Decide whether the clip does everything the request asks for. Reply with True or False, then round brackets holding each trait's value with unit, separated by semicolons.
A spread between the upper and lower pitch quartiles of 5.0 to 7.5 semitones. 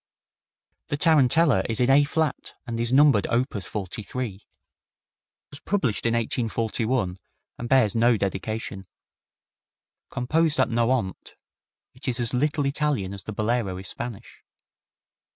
False (4.0 semitones)